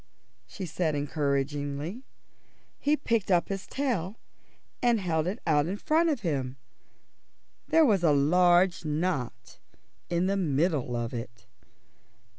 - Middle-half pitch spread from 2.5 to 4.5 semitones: No, wide, 5.4 semitones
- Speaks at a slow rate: Yes, slow, 125 wpm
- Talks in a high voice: No, medium, 170 Hz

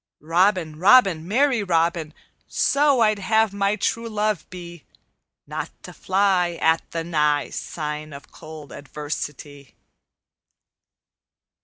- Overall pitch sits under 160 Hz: No, medium, 175 Hz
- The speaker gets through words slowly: Yes, slow, 110 wpm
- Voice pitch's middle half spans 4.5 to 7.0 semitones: Yes, average, 5.2 semitones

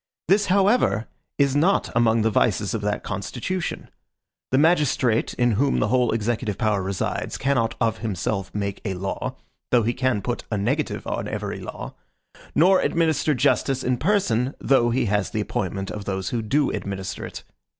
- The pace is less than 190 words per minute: Yes, average, 170 wpm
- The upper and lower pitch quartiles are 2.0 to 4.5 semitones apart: No, average, 5.1 semitones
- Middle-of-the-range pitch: No, low, 115 Hz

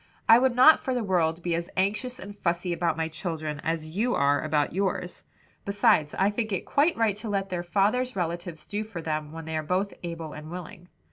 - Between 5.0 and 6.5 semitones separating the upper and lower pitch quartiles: No, average, 4.2 semitones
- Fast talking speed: Yes, fast, 215 wpm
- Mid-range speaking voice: Yes, medium, 180 Hz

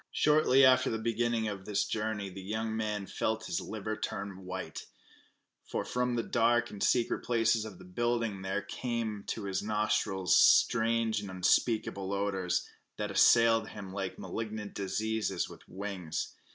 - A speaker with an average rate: Yes, average, 155 wpm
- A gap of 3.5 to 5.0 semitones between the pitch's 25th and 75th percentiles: No, average, 2.8 semitones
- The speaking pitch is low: Yes, low, 110 Hz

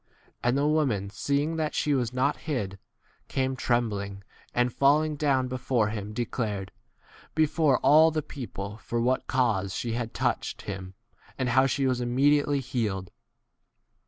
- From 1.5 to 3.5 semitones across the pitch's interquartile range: No, average, 4.7 semitones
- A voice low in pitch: Yes, low, 125 Hz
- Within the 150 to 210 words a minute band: Yes, average, 160 wpm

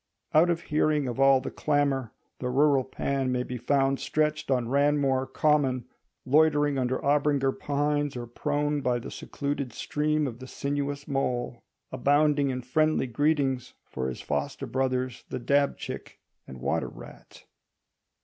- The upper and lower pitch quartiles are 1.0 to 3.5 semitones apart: Yes, narrow, 2.4 semitones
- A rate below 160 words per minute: Yes, average, 150 wpm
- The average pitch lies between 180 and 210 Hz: No, medium, 140 Hz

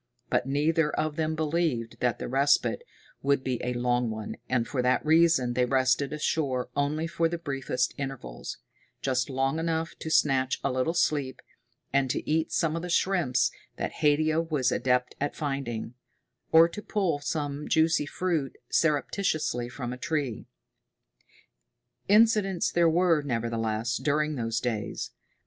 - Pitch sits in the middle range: Yes, medium, 145 Hz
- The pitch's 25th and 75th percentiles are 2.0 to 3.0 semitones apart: No, average, 4.2 semitones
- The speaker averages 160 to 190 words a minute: No, average, 150 wpm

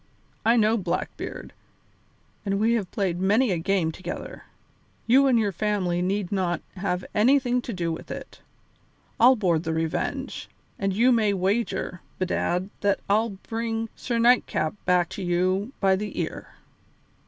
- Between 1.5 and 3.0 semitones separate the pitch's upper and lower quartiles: No, average, 4.0 semitones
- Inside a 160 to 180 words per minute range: No, average, 150 wpm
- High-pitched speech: Yes, high, 200 Hz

